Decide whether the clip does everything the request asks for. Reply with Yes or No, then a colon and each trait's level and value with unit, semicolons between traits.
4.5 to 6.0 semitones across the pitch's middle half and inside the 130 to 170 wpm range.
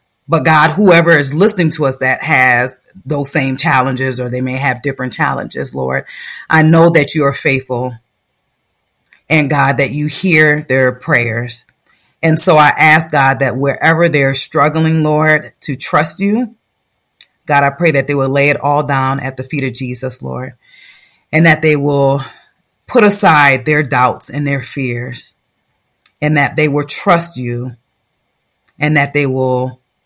No: average, 3.2 semitones; average, 165 wpm